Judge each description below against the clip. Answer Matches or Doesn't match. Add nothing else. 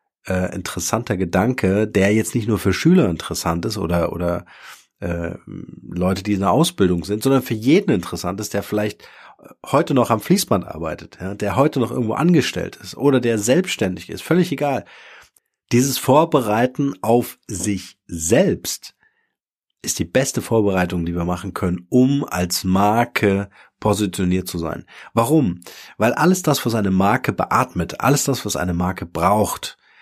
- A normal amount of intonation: Doesn't match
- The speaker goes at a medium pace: Matches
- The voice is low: Matches